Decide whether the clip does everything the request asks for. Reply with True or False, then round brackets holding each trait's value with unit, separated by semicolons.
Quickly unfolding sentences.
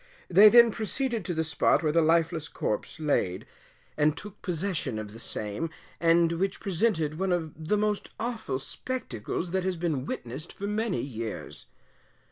False (160 wpm)